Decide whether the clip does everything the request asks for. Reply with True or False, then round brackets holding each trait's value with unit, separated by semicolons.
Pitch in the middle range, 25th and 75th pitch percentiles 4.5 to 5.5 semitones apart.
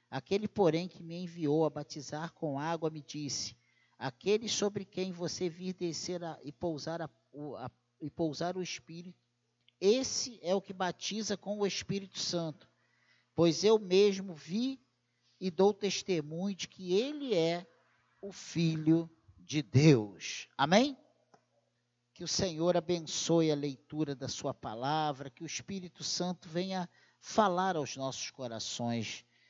True (165 Hz; 4.8 semitones)